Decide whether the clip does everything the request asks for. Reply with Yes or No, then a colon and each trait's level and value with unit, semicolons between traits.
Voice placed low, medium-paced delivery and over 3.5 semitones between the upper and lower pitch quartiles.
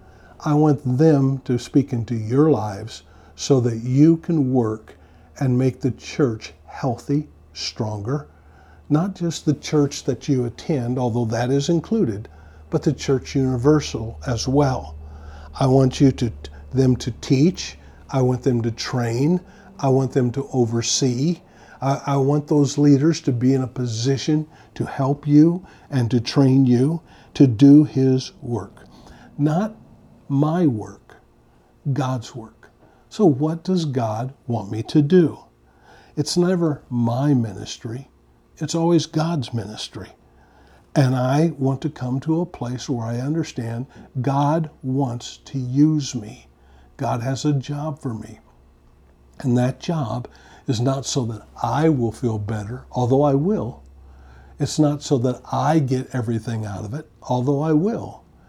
Yes: low, 130 Hz; average, 145 wpm; average, 4.5 semitones